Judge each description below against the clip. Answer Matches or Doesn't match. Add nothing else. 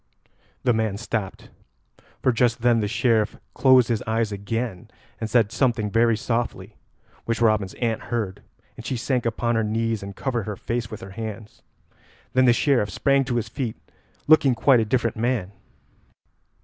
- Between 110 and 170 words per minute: Matches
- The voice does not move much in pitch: Matches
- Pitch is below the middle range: Matches